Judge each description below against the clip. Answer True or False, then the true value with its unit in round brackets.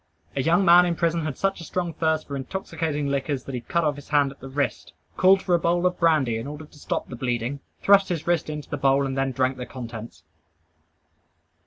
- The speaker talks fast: True (230 wpm)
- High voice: False (150 Hz)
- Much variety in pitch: False (4.1 semitones)